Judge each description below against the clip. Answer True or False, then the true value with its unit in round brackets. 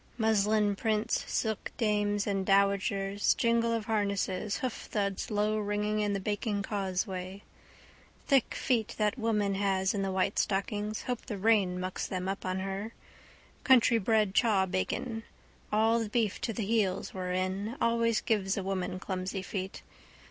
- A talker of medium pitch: False (205 Hz)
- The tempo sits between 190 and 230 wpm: False (140 wpm)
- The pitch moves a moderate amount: False (2.3 semitones)